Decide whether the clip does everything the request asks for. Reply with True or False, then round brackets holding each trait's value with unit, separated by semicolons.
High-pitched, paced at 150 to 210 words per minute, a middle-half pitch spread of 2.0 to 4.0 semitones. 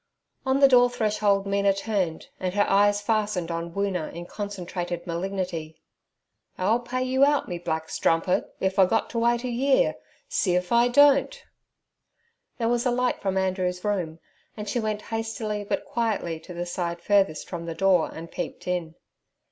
False (200 Hz; 170 wpm; 4.6 semitones)